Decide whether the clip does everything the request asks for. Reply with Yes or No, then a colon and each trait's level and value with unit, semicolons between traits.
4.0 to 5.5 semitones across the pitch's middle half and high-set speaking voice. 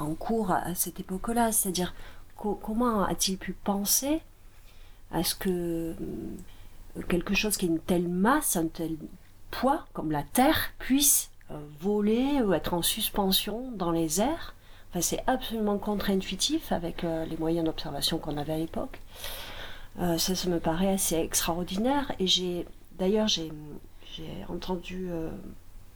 No: average, 4.4 semitones; medium, 180 Hz